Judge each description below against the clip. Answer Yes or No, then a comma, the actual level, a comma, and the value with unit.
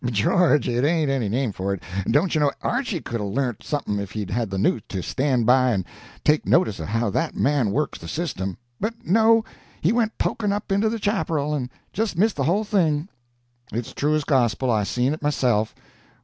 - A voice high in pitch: No, medium, 140 Hz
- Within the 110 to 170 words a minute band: No, average, 200 wpm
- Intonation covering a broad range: Yes, wide, 7.5 semitones